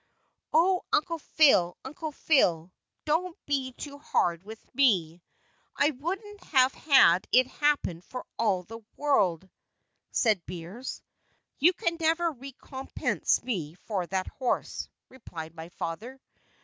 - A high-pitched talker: Yes, very high, 255 Hz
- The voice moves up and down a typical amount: No, wide, 8.7 semitones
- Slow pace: Yes, slow, 125 wpm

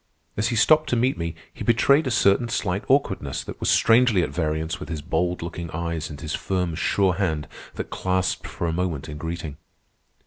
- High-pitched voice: No, very low, 90 Hz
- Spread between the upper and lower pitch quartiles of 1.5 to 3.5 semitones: No, average, 4.6 semitones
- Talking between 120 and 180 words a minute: No, average, 200 wpm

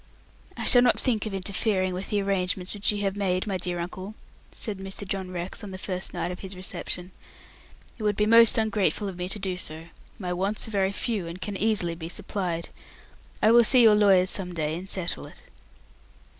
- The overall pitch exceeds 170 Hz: Yes, high, 190 Hz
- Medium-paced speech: No, fast, 210 wpm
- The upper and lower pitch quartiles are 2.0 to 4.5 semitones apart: Yes, narrow, 2.5 semitones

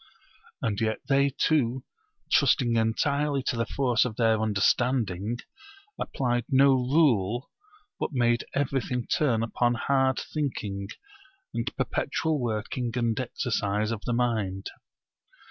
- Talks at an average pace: No, slow, 115 wpm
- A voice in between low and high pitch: No, low, 120 Hz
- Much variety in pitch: No, average, 3.2 semitones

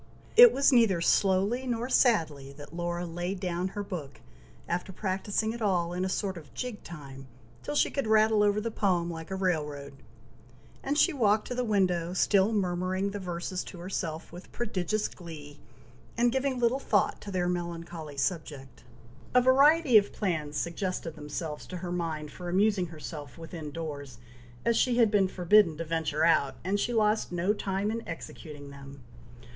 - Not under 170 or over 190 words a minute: Yes, average, 175 wpm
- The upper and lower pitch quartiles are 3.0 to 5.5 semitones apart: Yes, average, 4.5 semitones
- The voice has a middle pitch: Yes, medium, 180 Hz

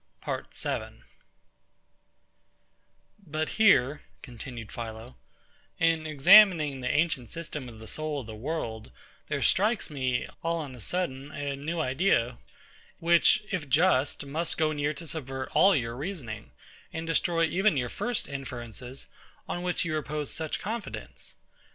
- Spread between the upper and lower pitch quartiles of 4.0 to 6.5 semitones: Yes, average, 4.6 semitones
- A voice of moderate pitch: Yes, medium, 150 Hz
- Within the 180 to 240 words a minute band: No, average, 140 wpm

